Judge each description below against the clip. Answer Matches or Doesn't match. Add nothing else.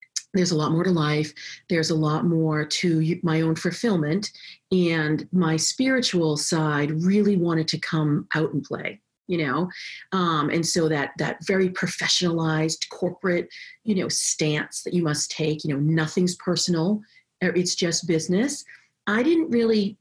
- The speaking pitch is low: Doesn't match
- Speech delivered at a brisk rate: Doesn't match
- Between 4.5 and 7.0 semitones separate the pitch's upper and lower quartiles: Doesn't match